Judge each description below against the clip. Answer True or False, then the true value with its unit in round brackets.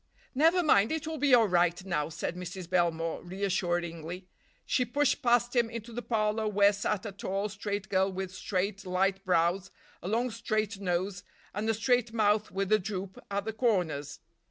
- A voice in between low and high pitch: False (200 Hz)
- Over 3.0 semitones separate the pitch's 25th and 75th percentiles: True (3.5 semitones)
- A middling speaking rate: True (180 wpm)